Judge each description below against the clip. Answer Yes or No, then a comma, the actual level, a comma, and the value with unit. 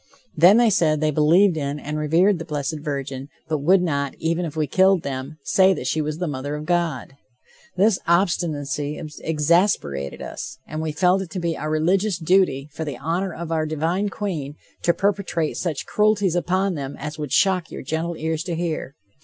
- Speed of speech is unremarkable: Yes, average, 190 wpm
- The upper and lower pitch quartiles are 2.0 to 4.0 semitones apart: Yes, average, 3.4 semitones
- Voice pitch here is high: No, medium, 160 Hz